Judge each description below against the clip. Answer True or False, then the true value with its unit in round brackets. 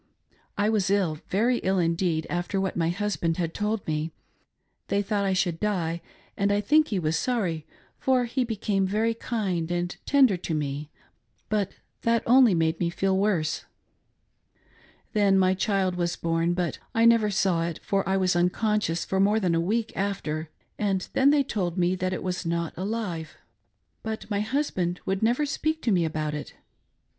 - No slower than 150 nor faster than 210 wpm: True (180 wpm)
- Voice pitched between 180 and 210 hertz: True (190 Hz)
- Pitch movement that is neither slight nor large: True (4.0 semitones)